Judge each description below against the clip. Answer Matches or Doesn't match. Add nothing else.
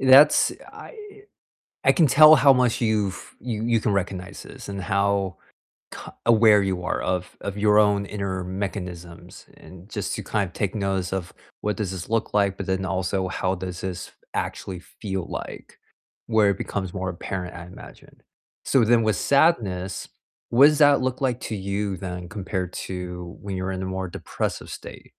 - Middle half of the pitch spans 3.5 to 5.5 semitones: Doesn't match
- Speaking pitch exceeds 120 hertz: Doesn't match